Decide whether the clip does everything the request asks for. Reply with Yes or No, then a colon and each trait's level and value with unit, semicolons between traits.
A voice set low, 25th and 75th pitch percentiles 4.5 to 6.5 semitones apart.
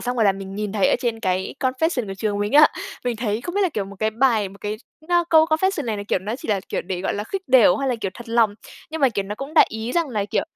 No: high, 225 Hz; average, 5.0 semitones